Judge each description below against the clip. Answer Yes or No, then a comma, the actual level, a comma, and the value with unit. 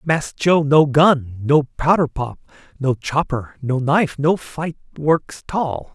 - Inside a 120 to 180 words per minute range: Yes, average, 150 wpm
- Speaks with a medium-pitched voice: Yes, medium, 145 Hz